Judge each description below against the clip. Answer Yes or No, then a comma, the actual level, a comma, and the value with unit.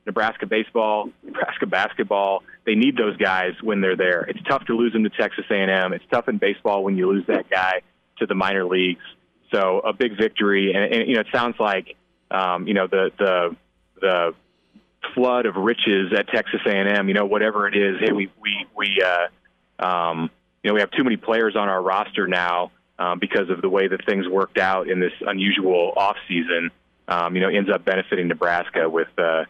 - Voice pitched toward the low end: Yes, very low, 95 Hz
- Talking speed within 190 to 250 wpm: Yes, fast, 205 wpm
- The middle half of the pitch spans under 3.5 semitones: Yes, average, 2.8 semitones